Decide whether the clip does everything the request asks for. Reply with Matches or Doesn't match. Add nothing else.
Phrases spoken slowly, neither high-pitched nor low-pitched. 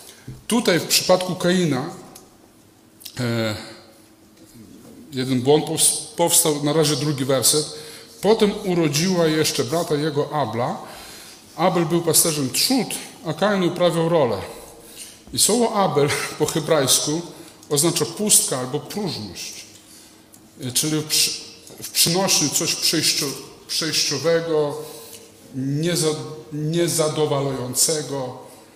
Matches